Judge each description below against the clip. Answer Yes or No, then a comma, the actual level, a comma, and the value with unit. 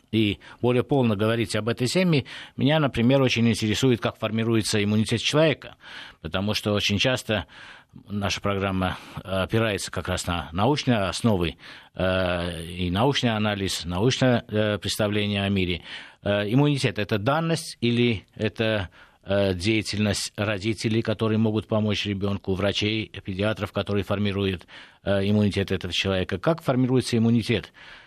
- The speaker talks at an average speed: Yes, average, 120 wpm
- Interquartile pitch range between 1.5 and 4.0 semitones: Yes, average, 3.2 semitones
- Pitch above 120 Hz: No, low, 105 Hz